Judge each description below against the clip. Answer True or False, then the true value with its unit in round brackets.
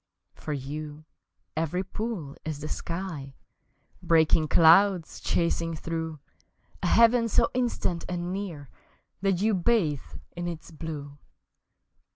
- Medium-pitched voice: True (165 Hz)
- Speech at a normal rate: False (115 wpm)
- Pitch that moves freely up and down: False (3.8 semitones)